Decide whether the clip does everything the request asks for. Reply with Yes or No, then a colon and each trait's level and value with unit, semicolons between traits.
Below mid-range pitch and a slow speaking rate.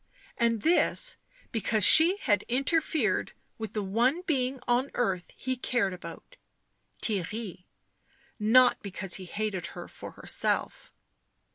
No: high, 230 Hz; slow, 125 wpm